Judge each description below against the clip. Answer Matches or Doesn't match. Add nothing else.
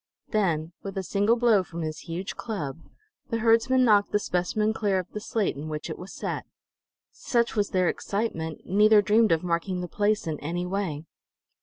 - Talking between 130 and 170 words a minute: Doesn't match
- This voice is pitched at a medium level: Doesn't match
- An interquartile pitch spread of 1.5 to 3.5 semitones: Doesn't match